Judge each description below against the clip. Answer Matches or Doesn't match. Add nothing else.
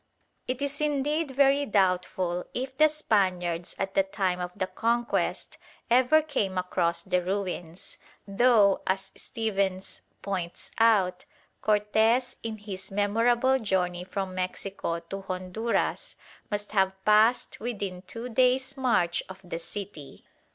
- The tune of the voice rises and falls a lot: Doesn't match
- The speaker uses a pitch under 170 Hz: Doesn't match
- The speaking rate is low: Matches